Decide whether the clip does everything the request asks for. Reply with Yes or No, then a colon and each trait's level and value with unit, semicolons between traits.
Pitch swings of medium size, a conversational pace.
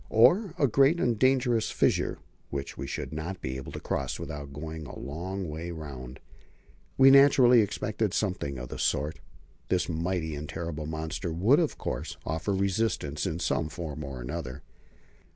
No: wide, 6.6 semitones; average, 165 wpm